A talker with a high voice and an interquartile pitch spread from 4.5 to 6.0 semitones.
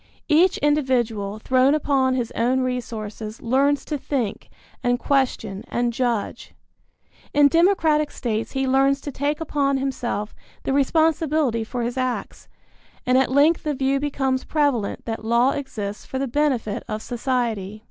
No: very high, 260 Hz; average, 3.4 semitones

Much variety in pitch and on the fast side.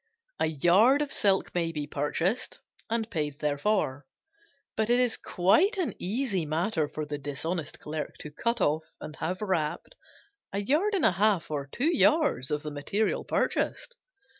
No: wide, 6.9 semitones; average, 165 wpm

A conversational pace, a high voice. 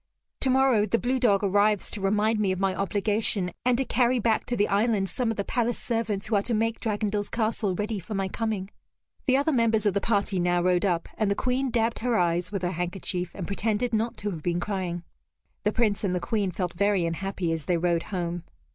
No: fast, 225 wpm; high, 205 Hz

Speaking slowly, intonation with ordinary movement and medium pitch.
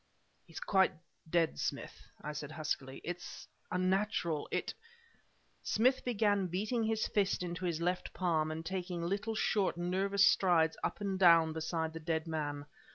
No: average, 155 wpm; average, 3.5 semitones; medium, 175 Hz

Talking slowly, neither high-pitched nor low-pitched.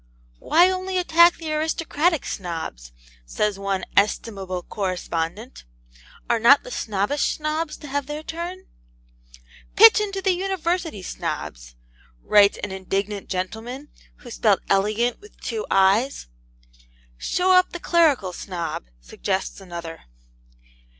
No: slow, 115 wpm; high, 235 Hz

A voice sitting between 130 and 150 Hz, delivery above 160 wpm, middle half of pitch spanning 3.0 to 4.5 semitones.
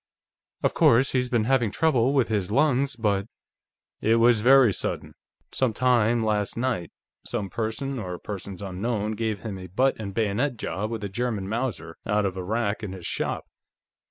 No: low, 110 Hz; average, 180 wpm; average, 3.5 semitones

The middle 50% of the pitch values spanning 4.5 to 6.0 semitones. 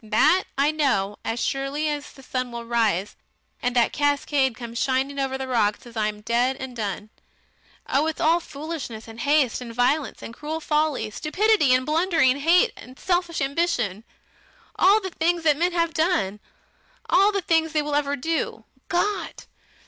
Yes: average, 5.2 semitones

